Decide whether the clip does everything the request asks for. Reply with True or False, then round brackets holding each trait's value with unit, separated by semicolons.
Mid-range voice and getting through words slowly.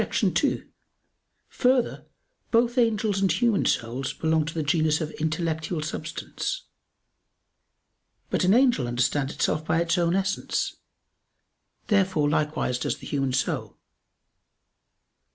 True (160 Hz; 115 wpm)